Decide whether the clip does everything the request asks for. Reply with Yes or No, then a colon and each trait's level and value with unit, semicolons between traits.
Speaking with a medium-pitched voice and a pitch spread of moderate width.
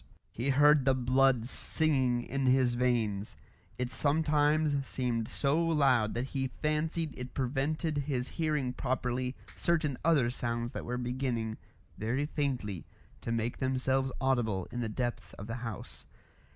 No: low, 130 Hz; average, 3.1 semitones